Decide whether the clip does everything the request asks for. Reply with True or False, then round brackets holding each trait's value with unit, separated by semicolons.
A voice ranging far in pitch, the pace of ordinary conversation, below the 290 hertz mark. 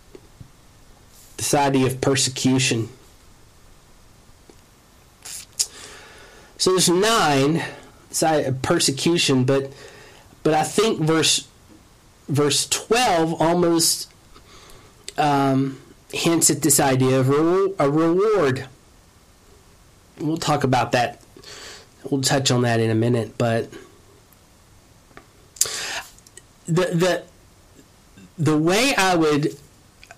False (5.9 semitones; 85 wpm; 135 Hz)